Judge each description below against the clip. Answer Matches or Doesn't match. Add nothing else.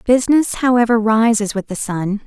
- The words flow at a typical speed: Matches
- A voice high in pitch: Matches